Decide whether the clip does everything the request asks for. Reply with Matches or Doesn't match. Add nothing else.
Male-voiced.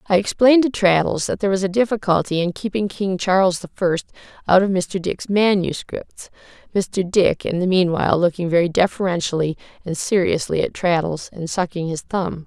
Doesn't match